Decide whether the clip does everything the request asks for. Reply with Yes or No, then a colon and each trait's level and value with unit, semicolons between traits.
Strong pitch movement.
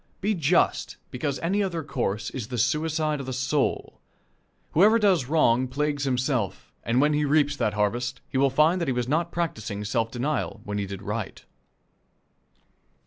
No: average, 4.6 semitones